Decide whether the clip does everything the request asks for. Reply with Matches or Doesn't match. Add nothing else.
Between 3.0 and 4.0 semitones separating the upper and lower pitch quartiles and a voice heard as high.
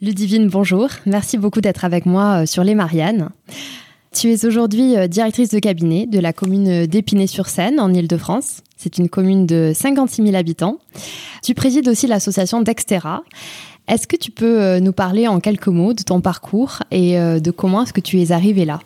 Matches